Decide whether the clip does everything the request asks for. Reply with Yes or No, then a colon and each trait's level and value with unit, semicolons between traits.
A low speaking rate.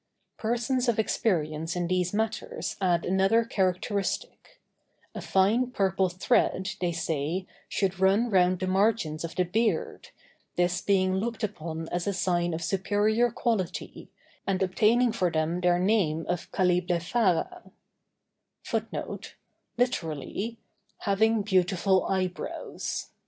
Yes: slow, 105 wpm